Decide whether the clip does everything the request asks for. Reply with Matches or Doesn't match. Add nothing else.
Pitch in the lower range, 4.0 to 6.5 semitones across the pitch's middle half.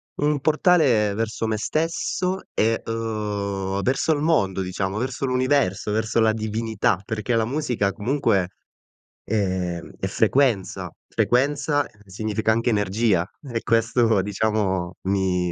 Matches